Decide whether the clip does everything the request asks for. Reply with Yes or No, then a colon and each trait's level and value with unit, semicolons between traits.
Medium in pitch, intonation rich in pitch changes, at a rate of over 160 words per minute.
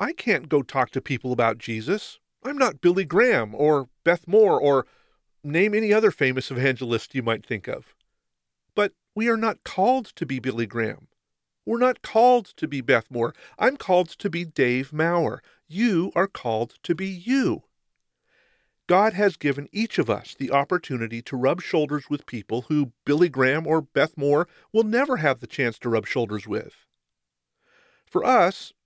Yes: medium, 145 Hz; wide, 7.8 semitones; average, 175 wpm